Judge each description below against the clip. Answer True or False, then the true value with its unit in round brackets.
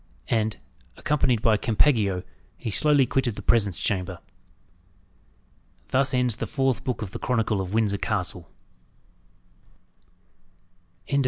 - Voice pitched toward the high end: False (115 Hz)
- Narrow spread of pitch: False (4.3 semitones)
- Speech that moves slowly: True (120 wpm)